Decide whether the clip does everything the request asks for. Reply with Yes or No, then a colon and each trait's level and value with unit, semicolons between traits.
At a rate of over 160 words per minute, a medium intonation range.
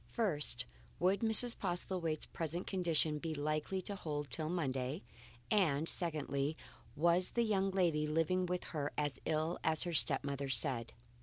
No: average, 155 wpm; average, 3.7 semitones